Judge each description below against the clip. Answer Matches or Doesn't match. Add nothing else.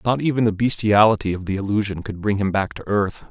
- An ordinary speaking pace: Doesn't match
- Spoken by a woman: Doesn't match